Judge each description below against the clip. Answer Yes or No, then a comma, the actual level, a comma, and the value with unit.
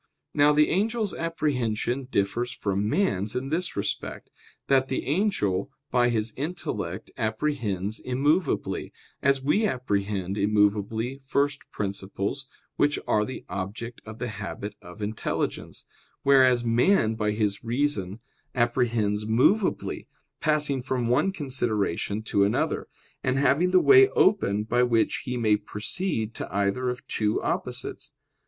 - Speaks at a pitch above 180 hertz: No, low, 120 Hz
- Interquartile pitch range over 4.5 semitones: Yes, average, 5.1 semitones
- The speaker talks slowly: Yes, slow, 130 wpm